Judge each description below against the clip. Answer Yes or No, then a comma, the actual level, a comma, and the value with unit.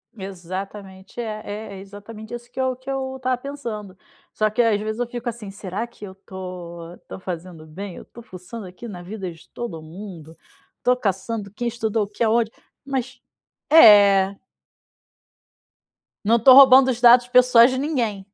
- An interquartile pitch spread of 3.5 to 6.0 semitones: Yes, average, 4.1 semitones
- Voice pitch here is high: Yes, high, 215 Hz